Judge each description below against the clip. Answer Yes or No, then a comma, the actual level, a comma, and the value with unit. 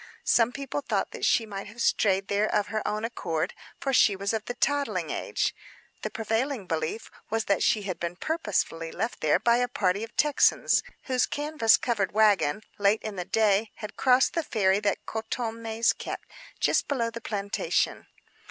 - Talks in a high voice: Yes, high, 220 Hz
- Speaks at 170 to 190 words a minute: Yes, average, 175 wpm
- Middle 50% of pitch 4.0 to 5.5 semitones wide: No, average, 3.2 semitones